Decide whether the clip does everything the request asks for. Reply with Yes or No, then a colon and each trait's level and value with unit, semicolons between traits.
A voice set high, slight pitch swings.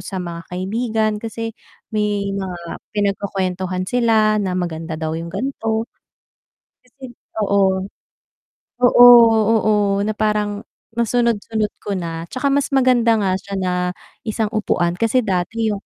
No: high, 205 Hz; average, 3.6 semitones